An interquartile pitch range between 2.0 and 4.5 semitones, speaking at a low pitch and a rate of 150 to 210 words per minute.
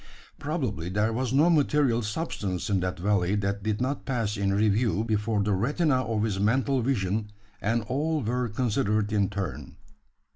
Yes: average, 4.2 semitones; low, 110 Hz; average, 160 wpm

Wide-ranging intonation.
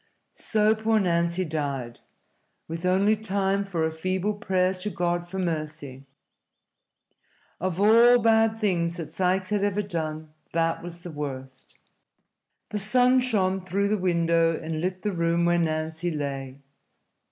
No: average, 3.8 semitones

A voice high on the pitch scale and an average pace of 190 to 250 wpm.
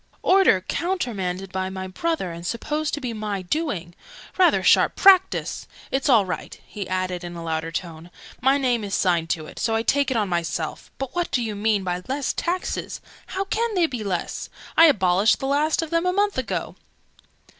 Yes: high, 220 Hz; average, 195 wpm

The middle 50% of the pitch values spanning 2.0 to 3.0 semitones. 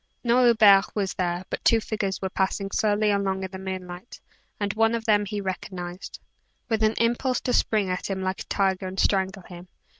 Yes: narrow, 2.4 semitones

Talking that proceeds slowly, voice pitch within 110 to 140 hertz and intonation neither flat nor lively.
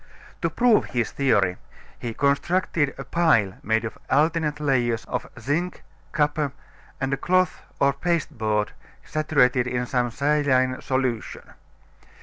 Yes: slow, 125 wpm; low, 135 Hz; average, 3.9 semitones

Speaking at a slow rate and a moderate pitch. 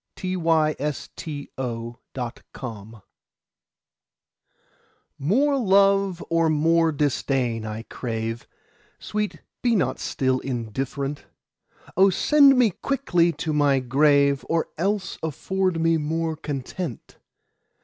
Yes: slow, 90 wpm; medium, 155 Hz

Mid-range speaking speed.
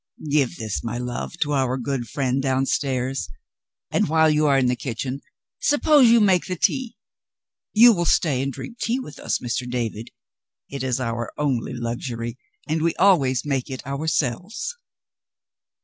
Yes: average, 160 wpm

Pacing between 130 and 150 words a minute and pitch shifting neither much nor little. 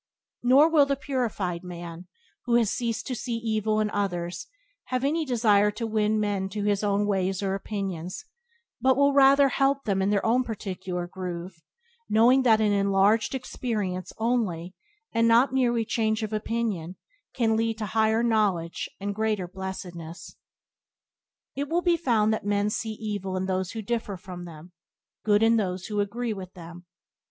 No: average, 165 wpm; average, 3.6 semitones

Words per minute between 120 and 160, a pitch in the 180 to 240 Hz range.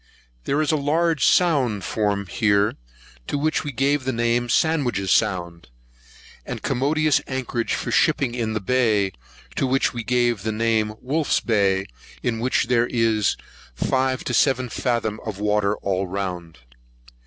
No: average, 155 wpm; low, 120 Hz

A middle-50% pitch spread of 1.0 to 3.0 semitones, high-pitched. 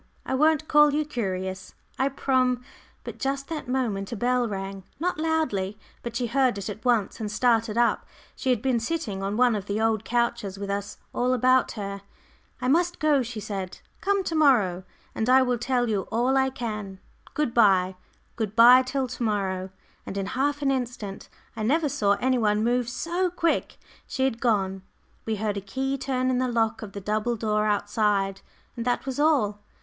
No: average, 4.3 semitones; high, 235 Hz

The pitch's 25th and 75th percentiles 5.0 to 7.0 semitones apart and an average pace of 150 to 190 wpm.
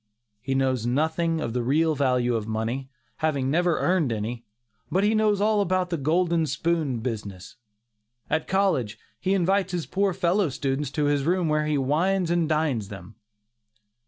Yes: wide, 5.6 semitones; average, 165 wpm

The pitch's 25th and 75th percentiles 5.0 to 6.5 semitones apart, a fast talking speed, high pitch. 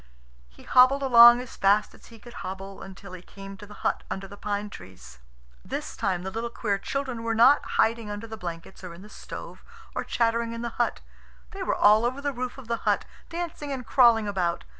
No: average, 3.7 semitones; fast, 215 wpm; high, 225 Hz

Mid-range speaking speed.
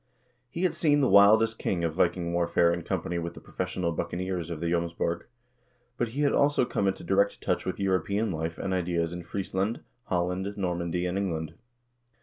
Yes: average, 180 wpm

